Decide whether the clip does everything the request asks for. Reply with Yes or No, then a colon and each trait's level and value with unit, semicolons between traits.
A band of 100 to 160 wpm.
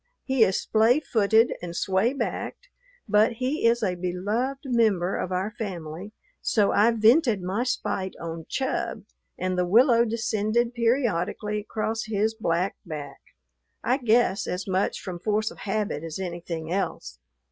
Yes: average, 145 wpm